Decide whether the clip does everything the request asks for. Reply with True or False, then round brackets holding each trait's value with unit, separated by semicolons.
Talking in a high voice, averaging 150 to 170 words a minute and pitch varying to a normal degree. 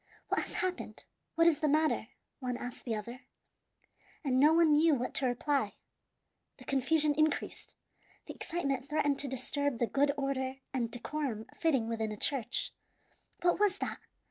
True (275 Hz; 160 wpm; 3.7 semitones)